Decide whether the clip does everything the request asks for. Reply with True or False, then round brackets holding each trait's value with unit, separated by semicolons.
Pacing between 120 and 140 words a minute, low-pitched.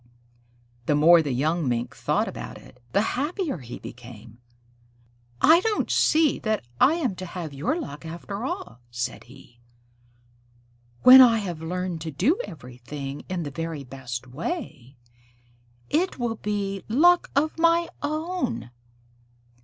False (135 wpm; 175 Hz)